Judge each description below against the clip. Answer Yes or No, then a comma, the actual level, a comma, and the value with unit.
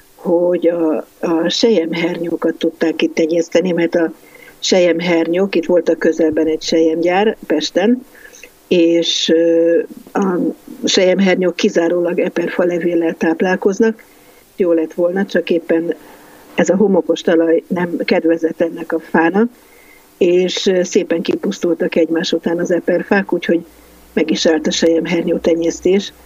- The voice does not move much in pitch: Yes, narrow, 1.6 semitones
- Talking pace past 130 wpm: No, average, 120 wpm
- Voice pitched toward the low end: No, medium, 170 Hz